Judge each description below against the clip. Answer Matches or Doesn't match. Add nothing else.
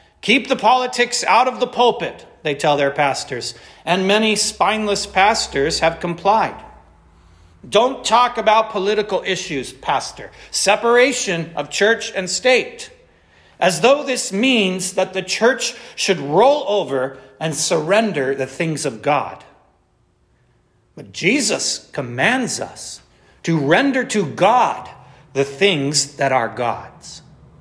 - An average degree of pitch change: Doesn't match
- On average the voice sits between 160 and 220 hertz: Matches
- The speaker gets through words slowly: Matches